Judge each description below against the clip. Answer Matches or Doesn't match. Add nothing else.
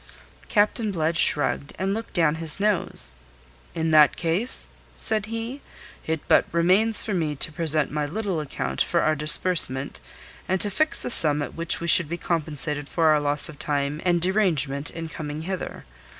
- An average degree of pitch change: Matches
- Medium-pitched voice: Matches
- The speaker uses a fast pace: Doesn't match